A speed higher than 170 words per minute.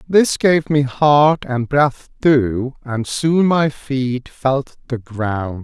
No: average, 150 wpm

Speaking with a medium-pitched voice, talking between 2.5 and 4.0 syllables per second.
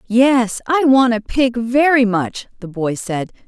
No: high, 235 Hz; 3.6 syllables/s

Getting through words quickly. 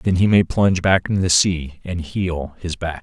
Yes: fast, 240 wpm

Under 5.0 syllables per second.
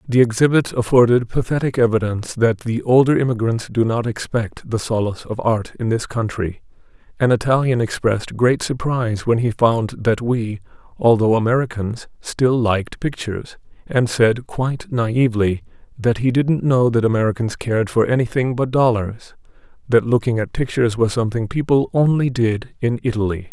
No: 5.2 syllables/s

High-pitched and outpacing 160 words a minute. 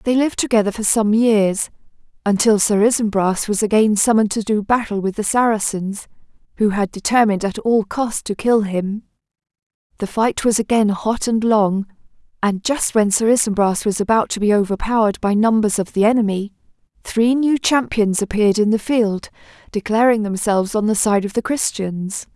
Yes: high, 215 Hz; average, 170 wpm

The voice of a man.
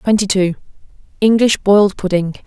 No: female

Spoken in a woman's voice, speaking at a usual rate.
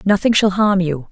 No: female; fast, 215 wpm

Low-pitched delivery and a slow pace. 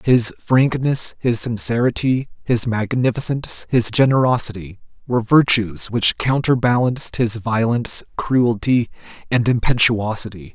Yes: low, 120 Hz; slow, 95 wpm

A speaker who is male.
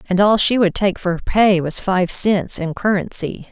No: female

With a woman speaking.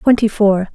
Yes: female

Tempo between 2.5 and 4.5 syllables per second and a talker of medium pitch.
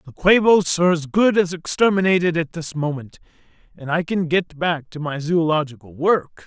No: 5.0 syllables/s; medium, 165 Hz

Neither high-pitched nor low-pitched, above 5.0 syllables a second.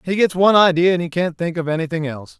Yes: medium, 170 Hz; 7.1 syllables/s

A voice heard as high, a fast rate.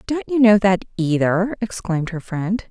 No: high, 200 Hz; average, 175 wpm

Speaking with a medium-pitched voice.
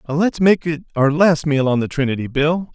Yes: medium, 150 Hz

